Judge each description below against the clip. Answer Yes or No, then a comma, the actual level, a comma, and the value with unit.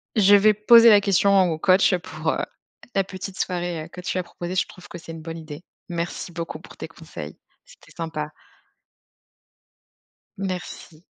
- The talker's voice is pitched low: No, medium, 180 Hz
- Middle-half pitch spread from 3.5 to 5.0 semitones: No, average, 2.9 semitones